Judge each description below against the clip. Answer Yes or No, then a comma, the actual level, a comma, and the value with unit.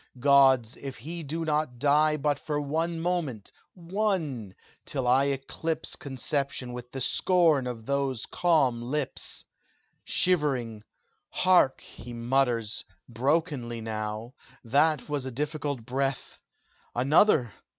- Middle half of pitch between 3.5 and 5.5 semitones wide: Yes, average, 4.0 semitones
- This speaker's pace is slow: Yes, slow, 115 wpm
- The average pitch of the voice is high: No, medium, 140 Hz